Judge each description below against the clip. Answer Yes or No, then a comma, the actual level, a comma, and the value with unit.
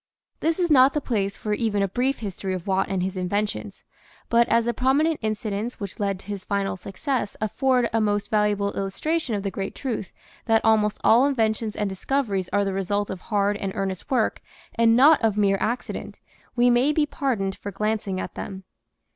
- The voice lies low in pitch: No, high, 210 Hz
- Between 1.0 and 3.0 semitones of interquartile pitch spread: No, average, 3.6 semitones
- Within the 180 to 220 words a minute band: Yes, average, 195 wpm